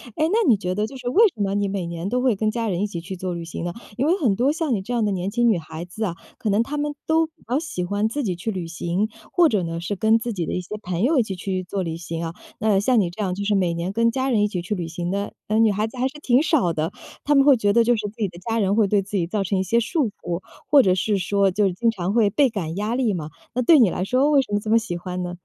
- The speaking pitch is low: No, high, 205 Hz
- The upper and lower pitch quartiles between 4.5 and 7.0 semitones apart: Yes, average, 4.8 semitones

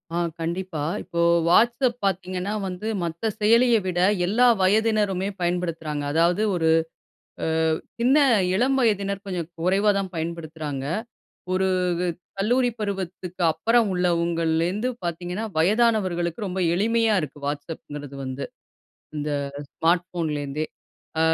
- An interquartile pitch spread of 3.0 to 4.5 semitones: Yes, average, 4.2 semitones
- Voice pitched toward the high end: No, medium, 180 Hz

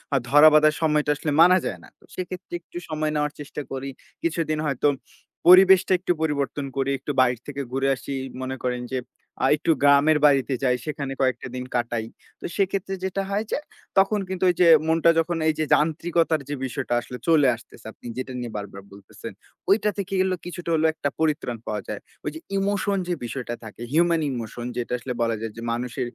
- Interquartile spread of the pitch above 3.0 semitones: Yes, average, 5.1 semitones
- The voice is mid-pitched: Yes, medium, 150 Hz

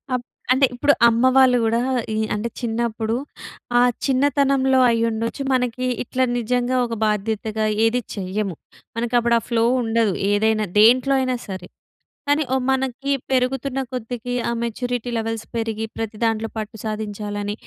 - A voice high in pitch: Yes, high, 230 Hz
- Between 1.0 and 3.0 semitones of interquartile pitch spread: Yes, narrow, 2.6 semitones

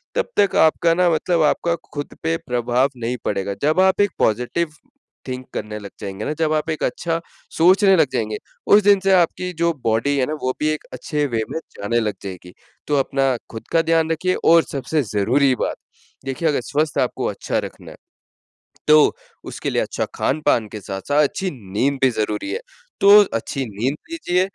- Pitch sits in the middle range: Yes, medium, 145 Hz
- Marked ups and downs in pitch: Yes, wide, 5.7 semitones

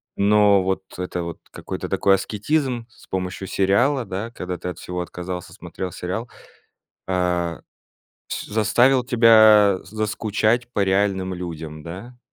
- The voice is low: Yes, low, 100 Hz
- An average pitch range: Yes, average, 3.5 semitones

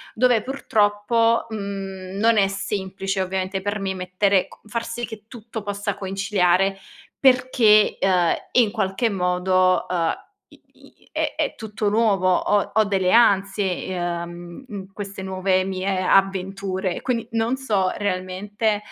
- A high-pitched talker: Yes, high, 195 Hz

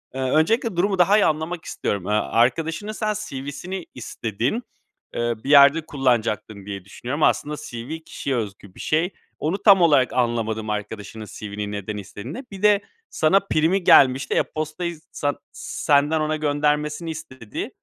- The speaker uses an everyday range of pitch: No, wide, 6.5 semitones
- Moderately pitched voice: Yes, medium, 145 Hz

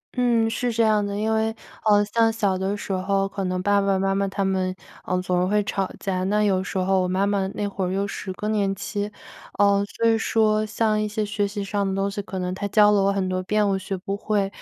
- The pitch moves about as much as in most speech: No, narrow, 1.7 semitones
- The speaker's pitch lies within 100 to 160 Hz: No, high, 200 Hz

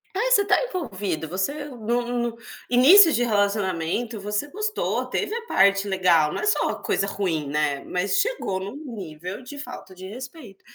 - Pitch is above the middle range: Yes, high, 205 Hz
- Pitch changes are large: Yes, wide, 7.4 semitones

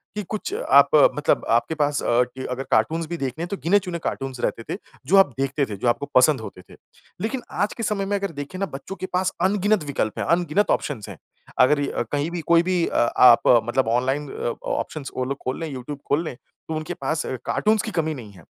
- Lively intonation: Yes, wide, 6.1 semitones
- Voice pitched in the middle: Yes, medium, 155 Hz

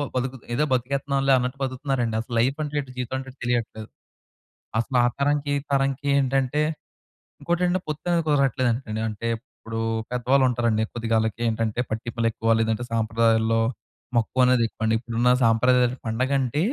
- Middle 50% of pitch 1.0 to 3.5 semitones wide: Yes, average, 3.1 semitones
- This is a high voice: No, low, 125 Hz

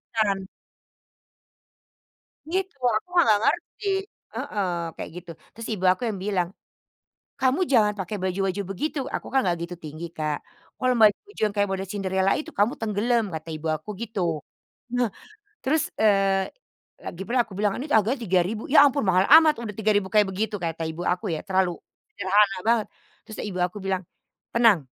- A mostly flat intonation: No, average, 3.6 semitones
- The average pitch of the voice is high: Yes, high, 205 Hz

